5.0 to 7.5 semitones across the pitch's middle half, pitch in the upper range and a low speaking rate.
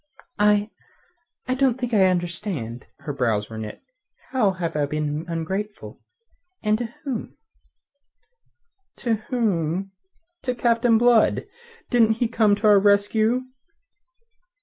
Yes: wide, 5.5 semitones; high, 210 Hz; slow, 120 wpm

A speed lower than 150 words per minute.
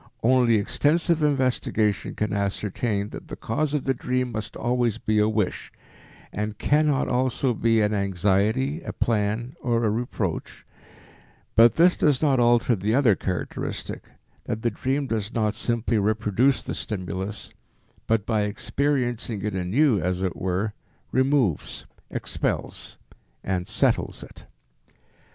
Yes: slow, 135 wpm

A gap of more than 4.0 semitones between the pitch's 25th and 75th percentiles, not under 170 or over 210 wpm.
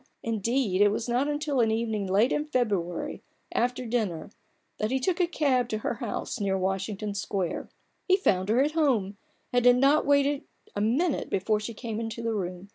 Yes: average, 4.7 semitones; average, 190 wpm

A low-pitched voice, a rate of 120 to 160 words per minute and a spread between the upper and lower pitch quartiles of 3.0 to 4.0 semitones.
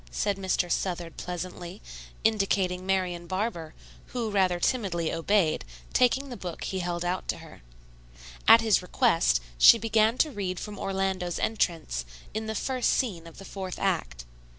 No: high, 190 Hz; average, 150 wpm; average, 3.7 semitones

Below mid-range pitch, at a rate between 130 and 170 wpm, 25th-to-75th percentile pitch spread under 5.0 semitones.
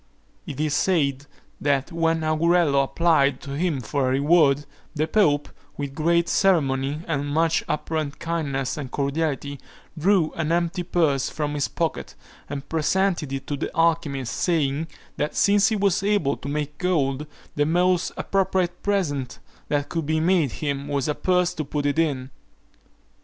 No: medium, 155 Hz; average, 160 wpm; average, 3.2 semitones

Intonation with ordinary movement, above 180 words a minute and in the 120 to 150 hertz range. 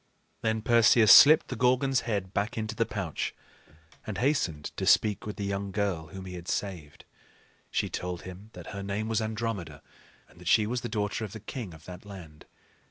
No: average, 3.5 semitones; average, 195 wpm; low, 105 Hz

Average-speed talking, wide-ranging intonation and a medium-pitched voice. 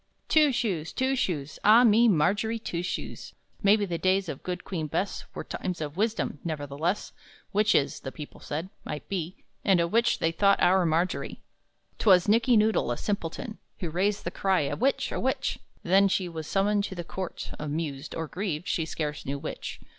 No: average, 185 wpm; average, 4.5 semitones; medium, 180 Hz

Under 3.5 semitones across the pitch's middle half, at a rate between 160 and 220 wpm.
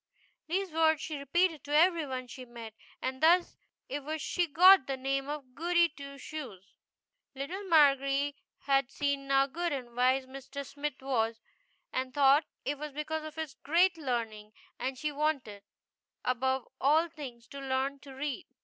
Yes: average, 3.0 semitones; average, 165 wpm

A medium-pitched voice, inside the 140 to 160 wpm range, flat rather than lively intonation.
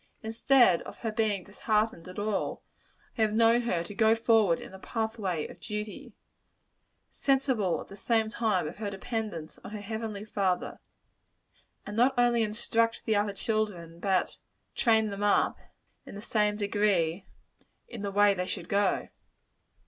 No: high, 210 Hz; average, 155 wpm; narrow, 2.2 semitones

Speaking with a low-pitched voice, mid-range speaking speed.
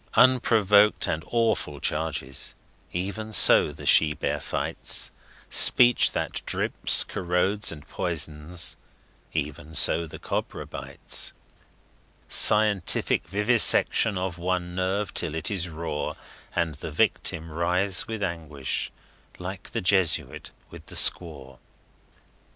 No: very low, 90 Hz; slow, 110 wpm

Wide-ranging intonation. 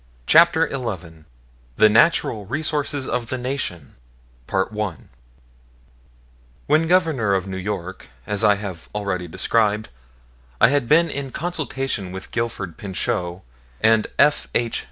Yes: wide, 6.7 semitones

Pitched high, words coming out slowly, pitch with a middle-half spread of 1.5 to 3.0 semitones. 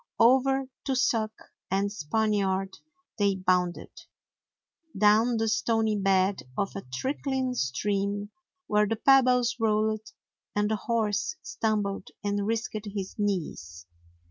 Yes: high, 210 Hz; slow, 110 wpm; narrow, 2.5 semitones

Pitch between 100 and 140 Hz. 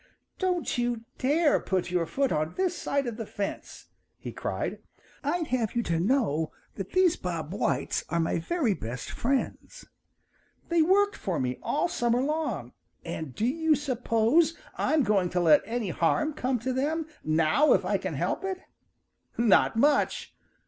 No: high, 240 Hz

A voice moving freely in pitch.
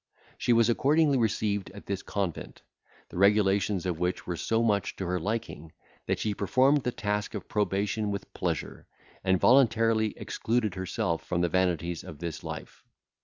No: average, 3.7 semitones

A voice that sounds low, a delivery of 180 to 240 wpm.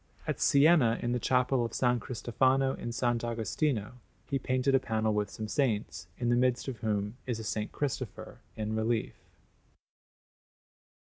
No: low, 120 Hz; average, 155 wpm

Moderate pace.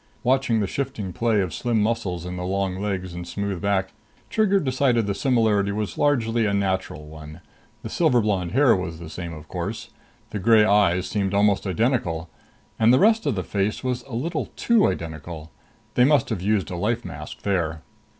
Yes: average, 190 wpm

